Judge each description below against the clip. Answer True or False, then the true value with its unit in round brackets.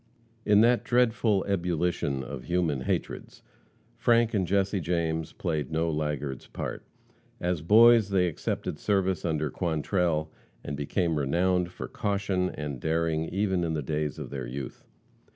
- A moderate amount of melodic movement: True (4.3 semitones)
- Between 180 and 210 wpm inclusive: False (140 wpm)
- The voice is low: True (85 Hz)